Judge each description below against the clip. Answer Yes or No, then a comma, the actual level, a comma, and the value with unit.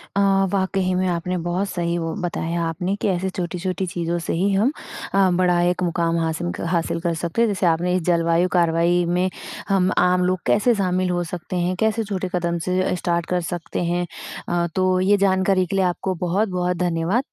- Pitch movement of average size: No, narrow, 1.5 semitones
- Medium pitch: Yes, medium, 180 Hz